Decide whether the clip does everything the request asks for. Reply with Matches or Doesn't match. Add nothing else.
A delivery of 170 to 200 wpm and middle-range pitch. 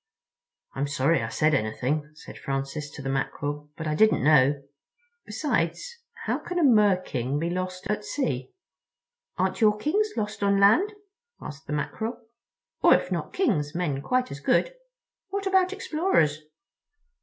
Doesn't match